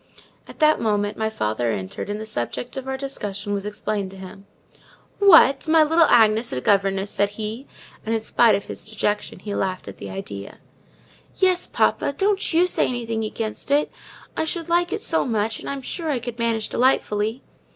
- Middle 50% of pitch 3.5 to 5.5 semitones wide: Yes, average, 5.2 semitones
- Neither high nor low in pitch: No, high, 220 Hz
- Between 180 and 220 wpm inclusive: Yes, average, 195 wpm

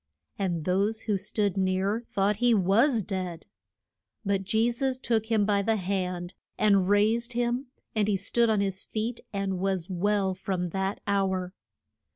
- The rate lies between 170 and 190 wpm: No, average, 160 wpm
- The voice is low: No, high, 200 Hz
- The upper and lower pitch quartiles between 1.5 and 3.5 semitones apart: Yes, narrow, 2.6 semitones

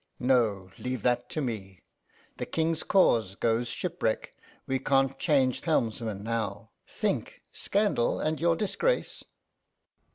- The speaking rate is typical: No, slow, 120 wpm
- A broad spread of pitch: Yes, wide, 6.0 semitones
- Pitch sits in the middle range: No, low, 125 Hz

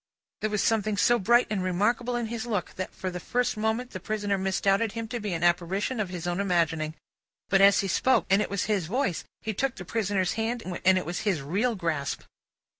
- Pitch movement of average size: Yes, average, 3.7 semitones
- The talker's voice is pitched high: Yes, high, 200 Hz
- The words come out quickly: Yes, fast, 215 wpm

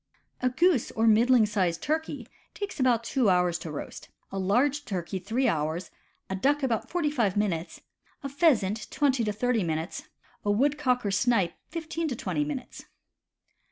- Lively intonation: Yes, wide, 6.6 semitones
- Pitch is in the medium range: No, high, 230 Hz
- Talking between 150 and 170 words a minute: Yes, average, 165 wpm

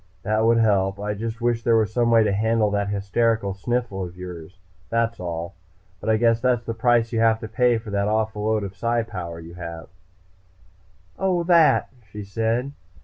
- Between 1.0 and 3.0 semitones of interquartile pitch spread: Yes, average, 2.7 semitones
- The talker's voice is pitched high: No, low, 110 Hz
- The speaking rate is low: No, average, 195 wpm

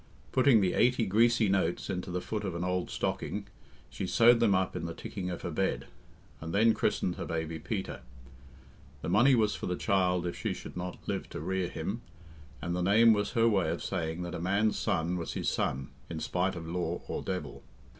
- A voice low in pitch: Yes, very low, 90 Hz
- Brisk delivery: Yes, fast, 210 wpm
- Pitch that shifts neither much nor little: Yes, average, 3.5 semitones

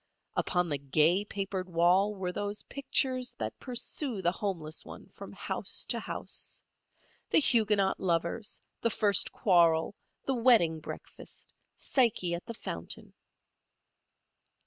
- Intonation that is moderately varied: Yes, average, 5.0 semitones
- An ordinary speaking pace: No, slow, 120 wpm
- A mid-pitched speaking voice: No, high, 195 Hz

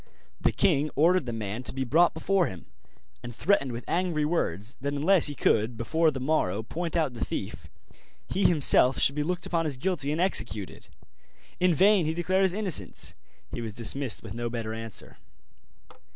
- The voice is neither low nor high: Yes, medium, 145 Hz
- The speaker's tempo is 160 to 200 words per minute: Yes, average, 180 wpm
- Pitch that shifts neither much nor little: No, wide, 6.6 semitones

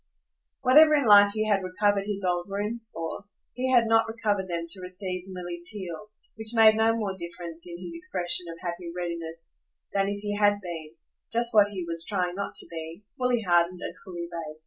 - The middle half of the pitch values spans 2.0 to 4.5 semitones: Yes, average, 3.6 semitones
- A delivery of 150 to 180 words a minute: No, average, 195 wpm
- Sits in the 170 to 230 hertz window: Yes, high, 190 Hz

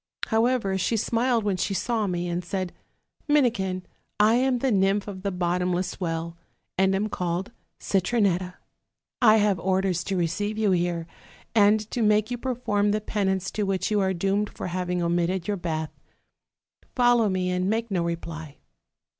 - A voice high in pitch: Yes, high, 195 Hz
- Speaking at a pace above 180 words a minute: No, average, 170 wpm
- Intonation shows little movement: No, average, 3.1 semitones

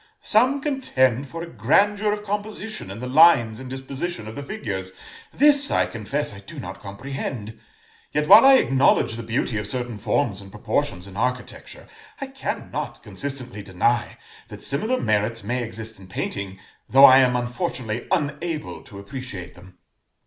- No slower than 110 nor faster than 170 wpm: Yes, average, 160 wpm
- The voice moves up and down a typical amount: No, wide, 7.8 semitones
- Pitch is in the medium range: No, low, 125 Hz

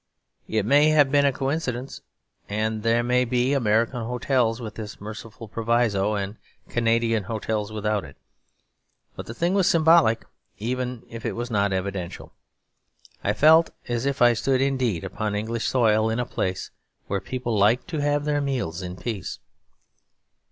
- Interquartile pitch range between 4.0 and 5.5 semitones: No, average, 3.4 semitones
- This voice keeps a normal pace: Yes, average, 160 wpm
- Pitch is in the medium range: No, low, 115 Hz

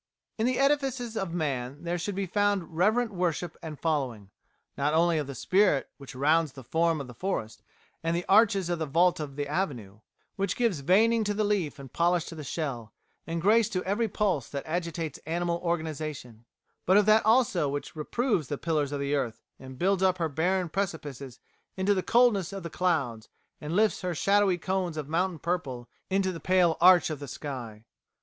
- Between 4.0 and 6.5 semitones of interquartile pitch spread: Yes, average, 5.0 semitones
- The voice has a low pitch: No, medium, 170 Hz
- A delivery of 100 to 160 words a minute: No, average, 195 wpm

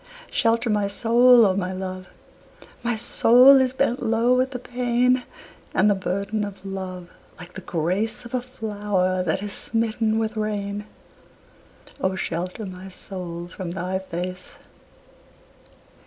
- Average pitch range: Yes, average, 4.0 semitones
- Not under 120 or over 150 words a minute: Yes, average, 140 wpm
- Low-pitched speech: No, high, 205 Hz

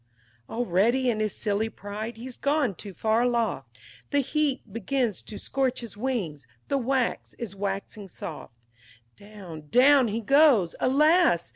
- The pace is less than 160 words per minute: Yes, average, 145 wpm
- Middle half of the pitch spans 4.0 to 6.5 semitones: Yes, average, 4.6 semitones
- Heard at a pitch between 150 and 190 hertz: No, high, 230 Hz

